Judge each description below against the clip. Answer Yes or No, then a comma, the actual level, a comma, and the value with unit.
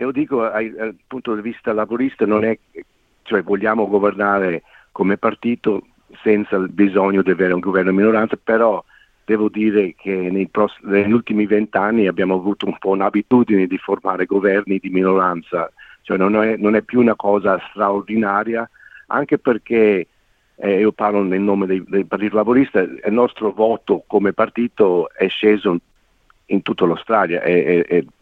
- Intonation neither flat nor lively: No, narrow, 2.2 semitones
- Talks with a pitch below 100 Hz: No, low, 105 Hz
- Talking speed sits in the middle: Yes, average, 155 wpm